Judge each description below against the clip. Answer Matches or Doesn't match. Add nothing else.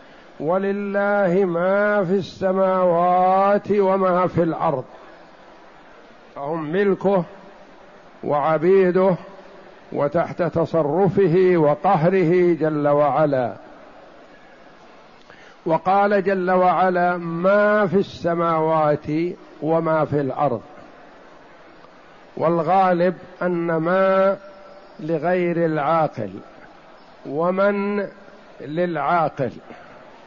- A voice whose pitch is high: Doesn't match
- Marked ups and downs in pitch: Doesn't match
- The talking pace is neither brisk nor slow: Doesn't match